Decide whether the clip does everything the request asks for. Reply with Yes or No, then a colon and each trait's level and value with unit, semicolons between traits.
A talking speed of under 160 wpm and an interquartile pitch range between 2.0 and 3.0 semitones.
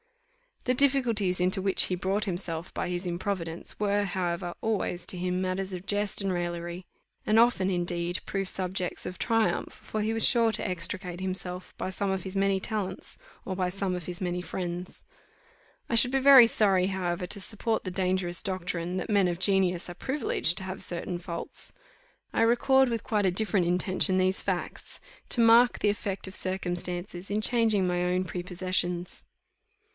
No: average, 175 wpm; narrow, 2.5 semitones